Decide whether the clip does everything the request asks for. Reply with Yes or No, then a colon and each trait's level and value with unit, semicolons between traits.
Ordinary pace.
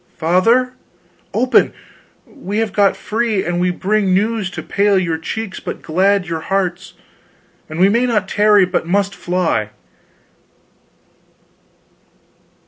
No: slow, 125 wpm